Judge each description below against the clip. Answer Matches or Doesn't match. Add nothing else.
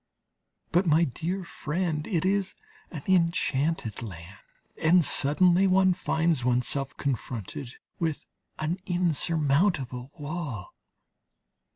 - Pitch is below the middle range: Doesn't match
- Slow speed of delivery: Matches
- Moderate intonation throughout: Matches